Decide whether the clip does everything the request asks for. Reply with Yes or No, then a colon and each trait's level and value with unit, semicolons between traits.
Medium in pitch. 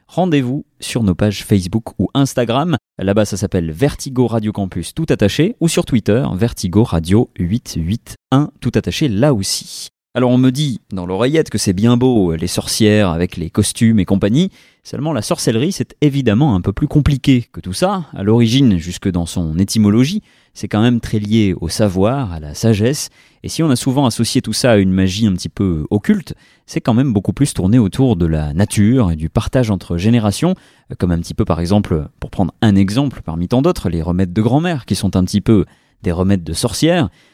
No: low, 110 Hz